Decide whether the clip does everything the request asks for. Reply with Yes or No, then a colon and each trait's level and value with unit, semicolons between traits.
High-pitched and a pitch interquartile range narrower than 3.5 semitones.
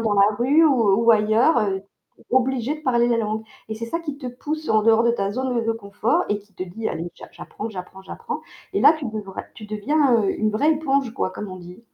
No: high, 230 Hz; average, 3.8 semitones